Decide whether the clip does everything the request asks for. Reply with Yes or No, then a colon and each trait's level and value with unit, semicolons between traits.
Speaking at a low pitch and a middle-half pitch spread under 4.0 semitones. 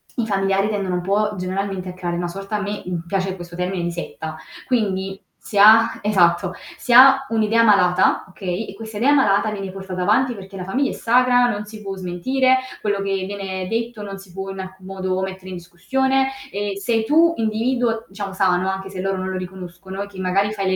No: high, 195 Hz; narrow, 2.6 semitones